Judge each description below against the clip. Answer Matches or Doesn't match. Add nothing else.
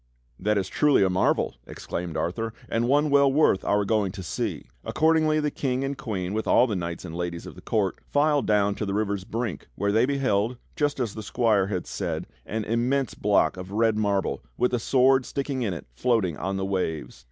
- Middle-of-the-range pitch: Doesn't match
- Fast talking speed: Matches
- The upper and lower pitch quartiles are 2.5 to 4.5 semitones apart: Doesn't match